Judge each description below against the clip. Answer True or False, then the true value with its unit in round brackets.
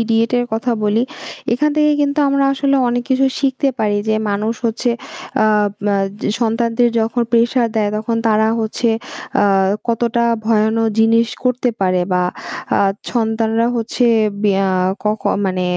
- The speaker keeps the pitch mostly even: True (2.1 semitones)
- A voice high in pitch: True (230 Hz)